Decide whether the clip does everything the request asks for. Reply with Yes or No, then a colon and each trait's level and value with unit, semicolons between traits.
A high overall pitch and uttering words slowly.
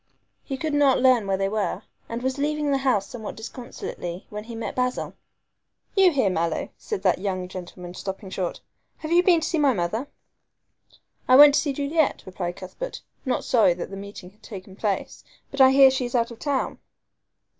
No: high, 240 Hz; average, 195 wpm